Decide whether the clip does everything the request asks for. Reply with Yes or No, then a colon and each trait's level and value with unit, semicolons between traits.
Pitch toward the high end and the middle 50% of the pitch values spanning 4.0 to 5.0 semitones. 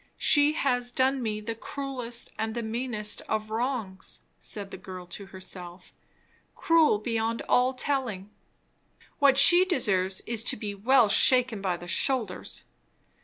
Yes: high, 230 Hz; average, 4.5 semitones